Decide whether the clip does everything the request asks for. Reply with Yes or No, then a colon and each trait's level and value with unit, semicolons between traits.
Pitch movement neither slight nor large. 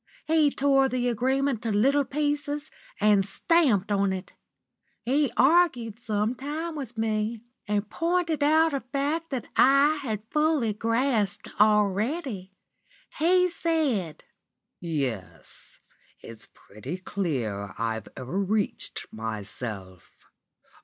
No: wide, 6.9 semitones